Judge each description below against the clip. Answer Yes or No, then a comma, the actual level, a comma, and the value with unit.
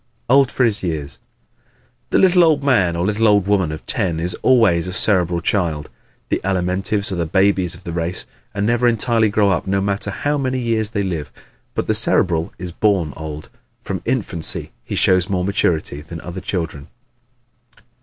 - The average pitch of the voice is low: Yes, very low, 95 Hz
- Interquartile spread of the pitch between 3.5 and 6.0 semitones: Yes, average, 4.2 semitones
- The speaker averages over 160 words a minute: Yes, average, 185 wpm